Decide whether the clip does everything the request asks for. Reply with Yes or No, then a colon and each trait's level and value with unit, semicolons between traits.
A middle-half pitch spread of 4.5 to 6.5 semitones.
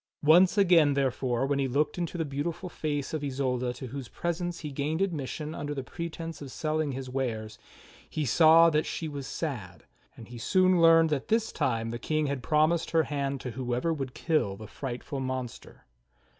No: average, 3.9 semitones